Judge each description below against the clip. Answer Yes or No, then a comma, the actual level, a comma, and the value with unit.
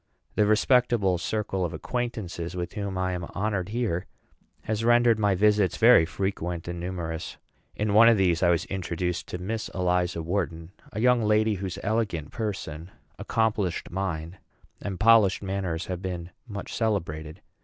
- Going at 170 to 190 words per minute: No, average, 155 wpm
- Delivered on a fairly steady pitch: No, average, 3.6 semitones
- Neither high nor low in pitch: No, very low, 95 Hz